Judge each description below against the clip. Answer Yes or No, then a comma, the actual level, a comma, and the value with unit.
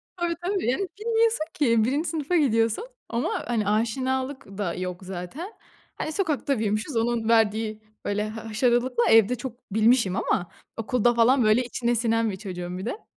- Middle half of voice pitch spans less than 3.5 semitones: No, average, 3.8 semitones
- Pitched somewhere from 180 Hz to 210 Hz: No, high, 235 Hz